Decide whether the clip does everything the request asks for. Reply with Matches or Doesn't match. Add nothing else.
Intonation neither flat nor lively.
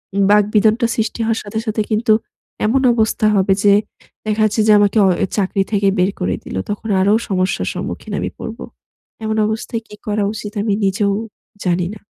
Doesn't match